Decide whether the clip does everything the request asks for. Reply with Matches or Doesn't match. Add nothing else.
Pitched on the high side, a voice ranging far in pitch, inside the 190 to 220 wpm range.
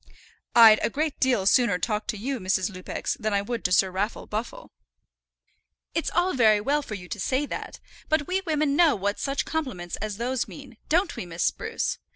Matches